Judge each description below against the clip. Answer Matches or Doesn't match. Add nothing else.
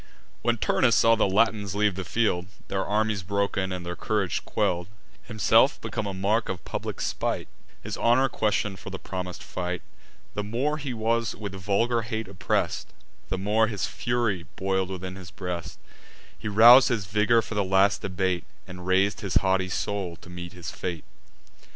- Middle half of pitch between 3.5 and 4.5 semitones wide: Doesn't match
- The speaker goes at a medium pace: Matches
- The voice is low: Matches